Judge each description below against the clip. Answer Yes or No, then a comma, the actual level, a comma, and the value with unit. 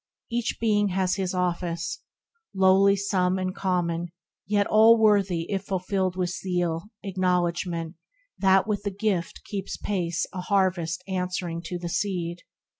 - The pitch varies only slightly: Yes, narrow, 2.1 semitones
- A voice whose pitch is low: No, medium, 185 Hz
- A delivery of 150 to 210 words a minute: No, slow, 135 wpm